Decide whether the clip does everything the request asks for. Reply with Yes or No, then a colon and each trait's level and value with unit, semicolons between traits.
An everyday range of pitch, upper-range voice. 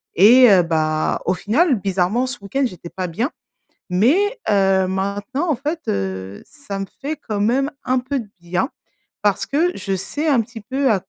No: wide, 6.3 semitones; high, 210 Hz